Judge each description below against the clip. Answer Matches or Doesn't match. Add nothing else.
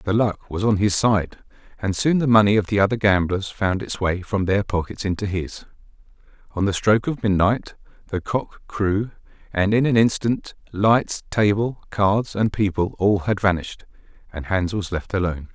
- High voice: Doesn't match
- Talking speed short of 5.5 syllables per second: Matches